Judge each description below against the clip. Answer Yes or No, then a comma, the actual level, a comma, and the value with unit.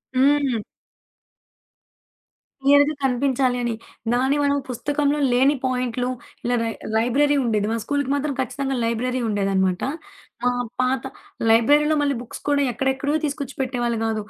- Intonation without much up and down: No, average, 3.1 semitones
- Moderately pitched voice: No, very high, 260 Hz